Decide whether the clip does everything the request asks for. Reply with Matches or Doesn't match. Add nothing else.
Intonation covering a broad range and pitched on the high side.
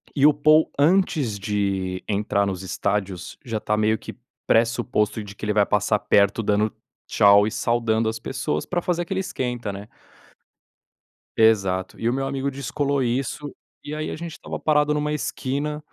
Doesn't match